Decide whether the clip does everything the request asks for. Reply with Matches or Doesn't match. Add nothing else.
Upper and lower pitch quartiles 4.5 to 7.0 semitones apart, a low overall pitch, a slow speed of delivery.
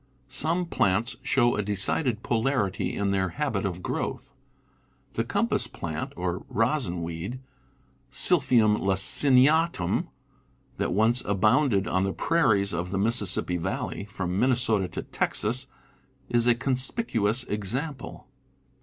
Matches